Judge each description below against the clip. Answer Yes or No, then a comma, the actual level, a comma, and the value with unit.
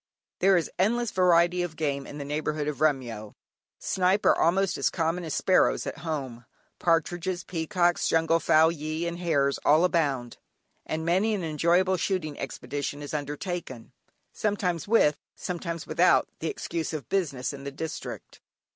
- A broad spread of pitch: No, average, 3.5 semitones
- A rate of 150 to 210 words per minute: Yes, average, 155 wpm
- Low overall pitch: No, medium, 165 Hz